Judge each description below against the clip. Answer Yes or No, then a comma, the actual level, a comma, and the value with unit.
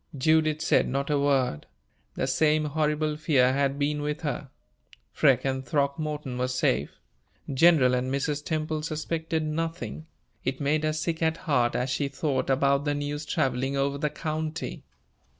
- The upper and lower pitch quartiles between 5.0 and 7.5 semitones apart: No, narrow, 2.4 semitones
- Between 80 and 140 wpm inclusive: No, average, 155 wpm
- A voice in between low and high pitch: Yes, medium, 145 Hz